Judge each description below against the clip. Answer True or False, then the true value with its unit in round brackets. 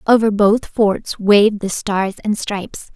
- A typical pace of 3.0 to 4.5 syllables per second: True (4.2 syllables/s)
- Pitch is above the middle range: True (205 Hz)